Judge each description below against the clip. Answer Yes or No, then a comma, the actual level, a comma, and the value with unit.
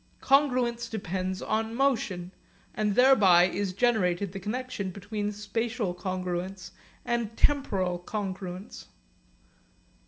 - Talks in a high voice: Yes, high, 205 Hz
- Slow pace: Yes, slow, 95 wpm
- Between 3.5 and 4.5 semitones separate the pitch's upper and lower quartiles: Yes, average, 4.2 semitones